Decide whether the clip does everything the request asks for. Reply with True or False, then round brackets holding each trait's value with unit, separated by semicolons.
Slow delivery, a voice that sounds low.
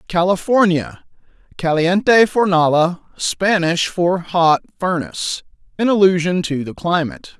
False (90 wpm; 175 Hz)